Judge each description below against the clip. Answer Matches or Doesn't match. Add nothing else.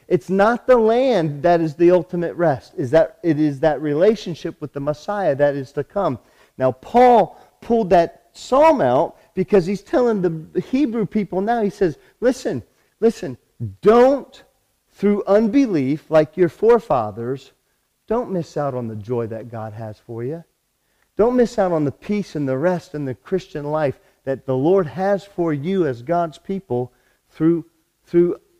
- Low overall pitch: Doesn't match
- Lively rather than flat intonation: Matches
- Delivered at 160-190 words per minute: Matches